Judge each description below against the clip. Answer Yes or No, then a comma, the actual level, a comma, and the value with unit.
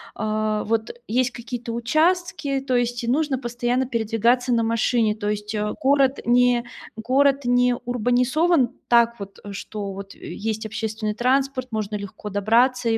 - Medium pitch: No, high, 240 Hz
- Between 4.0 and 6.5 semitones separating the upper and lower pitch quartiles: No, average, 2.9 semitones